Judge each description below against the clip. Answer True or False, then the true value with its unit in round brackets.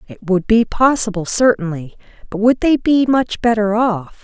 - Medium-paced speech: True (170 wpm)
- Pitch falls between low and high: False (215 Hz)